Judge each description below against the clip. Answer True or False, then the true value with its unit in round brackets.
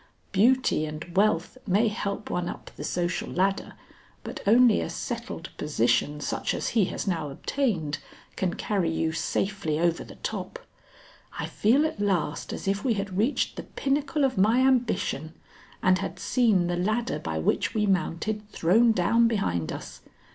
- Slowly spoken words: False (160 wpm)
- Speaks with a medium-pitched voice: False (195 Hz)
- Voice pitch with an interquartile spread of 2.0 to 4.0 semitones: False (5.3 semitones)